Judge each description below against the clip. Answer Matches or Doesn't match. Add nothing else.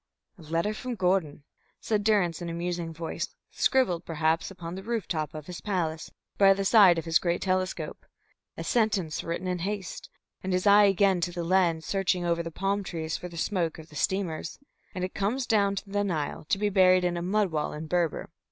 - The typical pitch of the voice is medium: Matches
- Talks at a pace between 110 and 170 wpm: Doesn't match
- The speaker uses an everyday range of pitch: Matches